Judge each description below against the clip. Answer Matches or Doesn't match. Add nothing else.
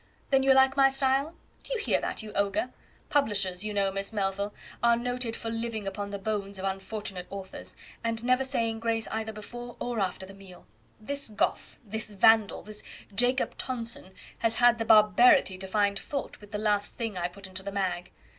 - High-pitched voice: Matches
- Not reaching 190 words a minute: Doesn't match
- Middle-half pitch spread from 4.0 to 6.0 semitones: Doesn't match